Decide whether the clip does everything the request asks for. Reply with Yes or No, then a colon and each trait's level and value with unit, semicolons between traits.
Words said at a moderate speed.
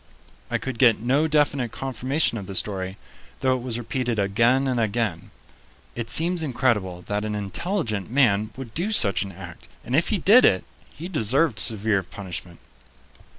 Yes: average, 165 wpm